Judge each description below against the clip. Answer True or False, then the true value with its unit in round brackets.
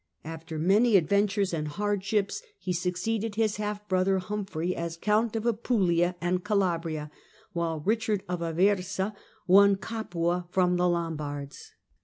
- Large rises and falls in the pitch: False (3.5 semitones)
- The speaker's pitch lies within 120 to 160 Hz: False (185 Hz)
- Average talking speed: False (130 wpm)